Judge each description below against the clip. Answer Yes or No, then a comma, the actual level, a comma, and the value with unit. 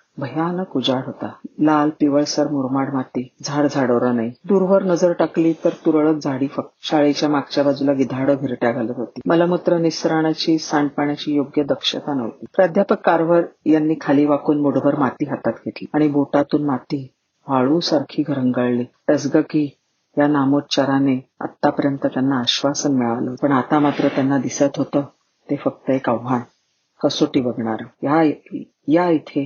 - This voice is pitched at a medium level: Yes, medium, 145 Hz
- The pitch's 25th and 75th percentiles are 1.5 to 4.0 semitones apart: Yes, narrow, 2.6 semitones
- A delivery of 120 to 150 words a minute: Yes, fast, 130 wpm